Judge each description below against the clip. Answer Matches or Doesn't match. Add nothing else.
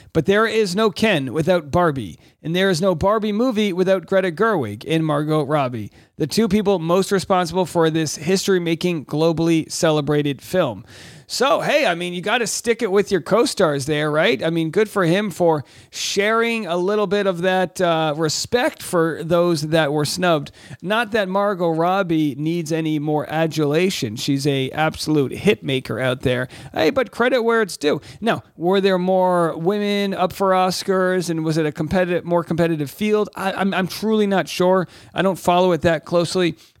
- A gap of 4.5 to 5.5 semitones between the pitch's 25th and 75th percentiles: Doesn't match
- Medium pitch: Matches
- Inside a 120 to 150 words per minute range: Doesn't match